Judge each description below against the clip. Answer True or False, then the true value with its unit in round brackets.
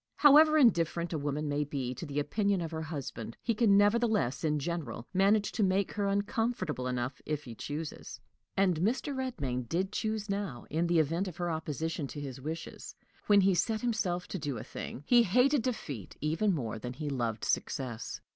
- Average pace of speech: True (190 wpm)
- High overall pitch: False (170 Hz)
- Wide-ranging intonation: True (6.2 semitones)